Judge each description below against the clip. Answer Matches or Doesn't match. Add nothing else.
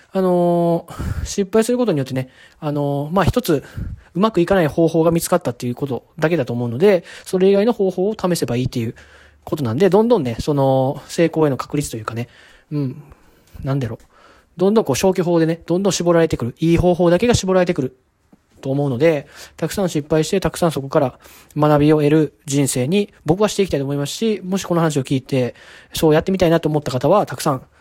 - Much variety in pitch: Doesn't match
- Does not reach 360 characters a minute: Doesn't match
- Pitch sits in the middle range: Matches